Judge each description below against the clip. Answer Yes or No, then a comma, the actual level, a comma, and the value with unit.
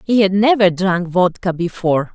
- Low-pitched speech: No, medium, 185 Hz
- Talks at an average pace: Yes, average, 170 wpm